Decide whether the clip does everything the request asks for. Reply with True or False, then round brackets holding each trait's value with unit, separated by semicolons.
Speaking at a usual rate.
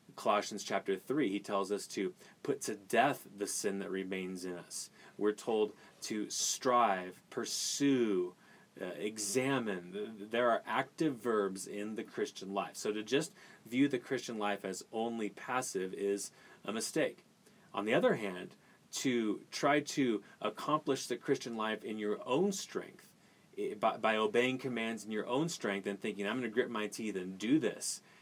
True (165 wpm)